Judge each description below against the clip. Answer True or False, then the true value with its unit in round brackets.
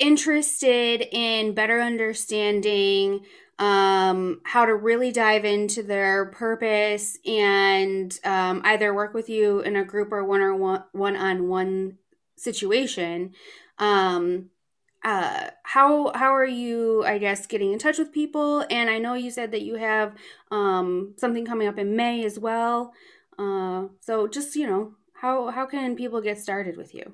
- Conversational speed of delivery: True (155 wpm)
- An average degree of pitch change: True (3.4 semitones)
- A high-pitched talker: True (215 Hz)